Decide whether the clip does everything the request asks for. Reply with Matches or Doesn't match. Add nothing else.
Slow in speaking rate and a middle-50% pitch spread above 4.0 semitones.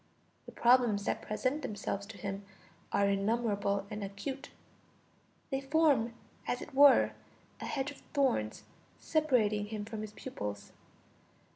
Matches